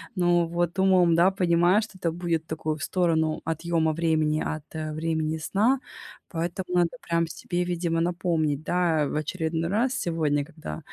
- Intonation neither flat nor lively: No, narrow, 1.9 semitones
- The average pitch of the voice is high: No, medium, 170 Hz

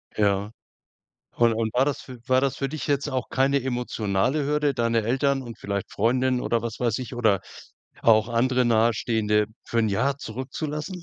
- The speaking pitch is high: No, low, 120 Hz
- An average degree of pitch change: Yes, average, 3.3 semitones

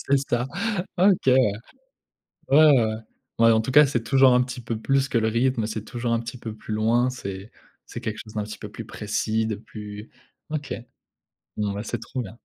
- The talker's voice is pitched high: No, low, 115 Hz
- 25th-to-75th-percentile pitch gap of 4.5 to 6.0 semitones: No, average, 3.0 semitones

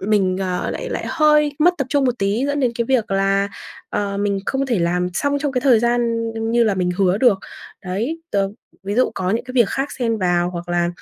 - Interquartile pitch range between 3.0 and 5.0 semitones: No, wide, 5.5 semitones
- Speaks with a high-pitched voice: Yes, high, 220 Hz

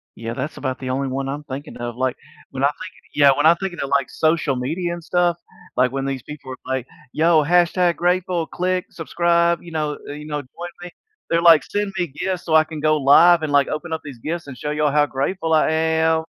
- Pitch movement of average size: Yes, average, 3.8 semitones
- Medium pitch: Yes, medium, 155 Hz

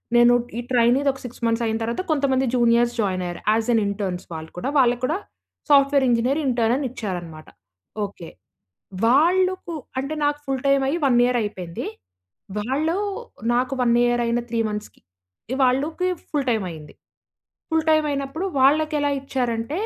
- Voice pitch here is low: No, very high, 250 Hz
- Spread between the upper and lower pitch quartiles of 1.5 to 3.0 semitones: No, average, 3.8 semitones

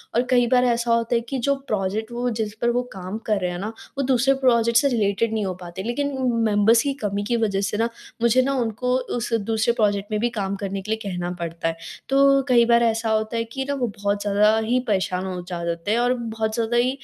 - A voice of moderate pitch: No, high, 225 Hz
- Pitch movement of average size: Yes, average, 3.0 semitones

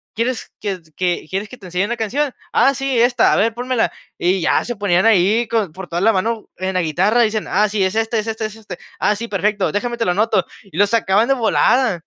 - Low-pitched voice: No, high, 215 Hz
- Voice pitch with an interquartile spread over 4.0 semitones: No, average, 3.4 semitones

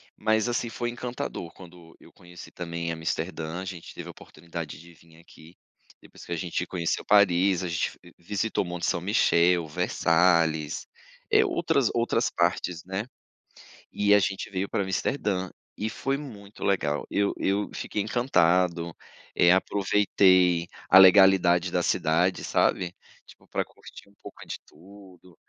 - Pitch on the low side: Yes, very low, 90 Hz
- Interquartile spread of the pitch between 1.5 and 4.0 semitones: Yes, average, 3.1 semitones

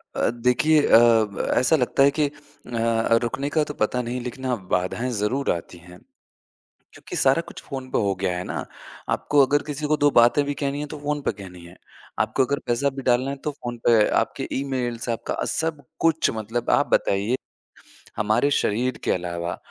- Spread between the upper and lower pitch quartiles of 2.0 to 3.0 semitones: No, average, 4.3 semitones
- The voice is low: Yes, low, 125 Hz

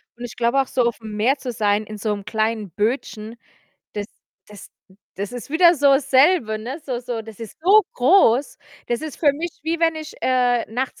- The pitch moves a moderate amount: Yes, average, 4.7 semitones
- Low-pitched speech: No, high, 245 Hz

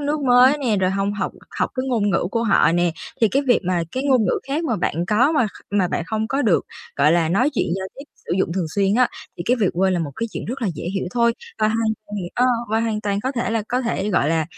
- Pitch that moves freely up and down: No, average, 4.7 semitones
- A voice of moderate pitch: No, high, 215 Hz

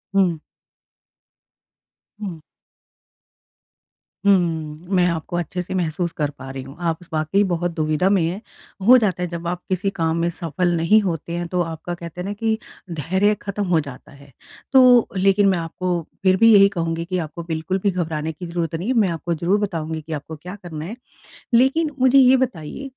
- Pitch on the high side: No, medium, 175 Hz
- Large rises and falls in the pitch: No, average, 3.4 semitones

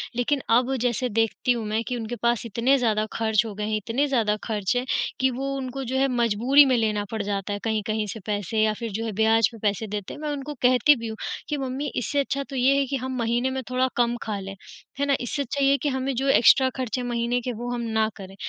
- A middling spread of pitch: Yes, average, 3.2 semitones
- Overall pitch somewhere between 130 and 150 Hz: No, high, 240 Hz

